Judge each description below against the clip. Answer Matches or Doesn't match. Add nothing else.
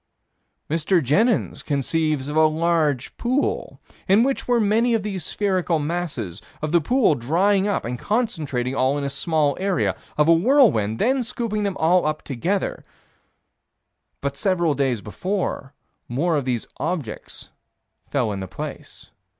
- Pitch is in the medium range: Matches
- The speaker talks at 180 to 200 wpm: Doesn't match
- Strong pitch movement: Matches